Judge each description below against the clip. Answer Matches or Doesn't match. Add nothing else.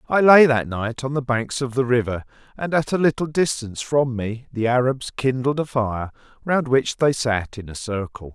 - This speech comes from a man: Matches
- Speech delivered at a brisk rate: Matches